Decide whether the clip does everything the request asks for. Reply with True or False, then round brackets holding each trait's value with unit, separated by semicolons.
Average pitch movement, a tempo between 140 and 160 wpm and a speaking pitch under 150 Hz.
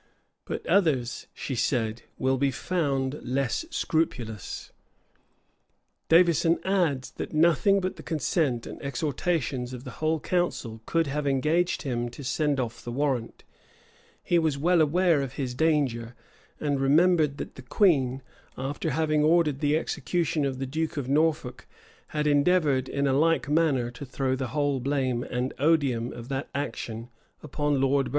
True (3.6 semitones; 155 wpm; 140 Hz)